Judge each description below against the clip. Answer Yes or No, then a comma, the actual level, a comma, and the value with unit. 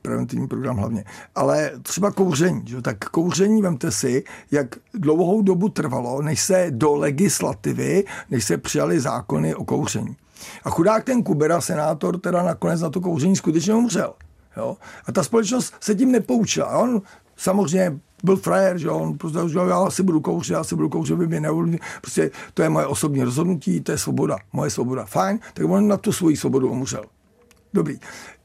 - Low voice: No, medium, 175 Hz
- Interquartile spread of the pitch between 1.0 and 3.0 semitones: No, average, 4.8 semitones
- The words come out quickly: Yes, fast, 175 wpm